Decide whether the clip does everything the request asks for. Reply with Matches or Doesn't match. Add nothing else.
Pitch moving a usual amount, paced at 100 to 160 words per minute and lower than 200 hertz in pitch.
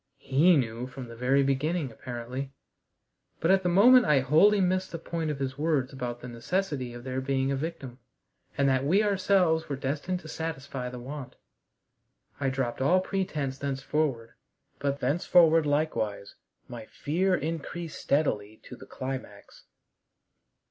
Matches